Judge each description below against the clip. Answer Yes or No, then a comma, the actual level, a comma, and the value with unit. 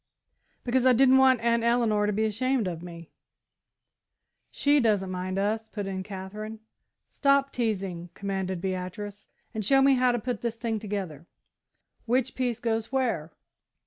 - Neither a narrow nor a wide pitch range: Yes, average, 4.3 semitones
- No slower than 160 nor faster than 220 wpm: No, average, 150 wpm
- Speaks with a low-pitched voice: No, high, 220 Hz